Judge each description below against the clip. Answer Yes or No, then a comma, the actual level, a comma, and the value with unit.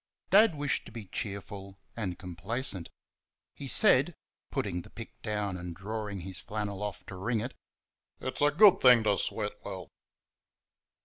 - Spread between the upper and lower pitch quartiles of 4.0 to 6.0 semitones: No, average, 3.6 semitones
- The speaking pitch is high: No, low, 105 Hz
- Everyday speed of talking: Yes, average, 150 wpm